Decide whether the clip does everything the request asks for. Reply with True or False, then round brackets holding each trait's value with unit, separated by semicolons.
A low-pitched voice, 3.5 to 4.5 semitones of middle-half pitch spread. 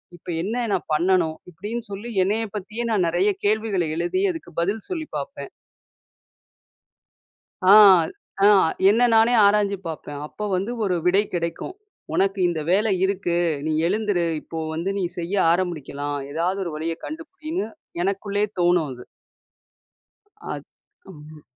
False (190 Hz; 4.0 semitones)